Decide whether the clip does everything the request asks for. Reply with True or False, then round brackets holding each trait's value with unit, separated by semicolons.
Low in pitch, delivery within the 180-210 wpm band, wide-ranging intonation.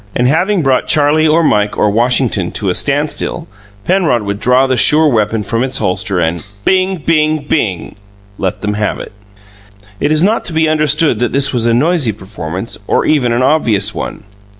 True (130 Hz; 185 wpm; 6.6 semitones)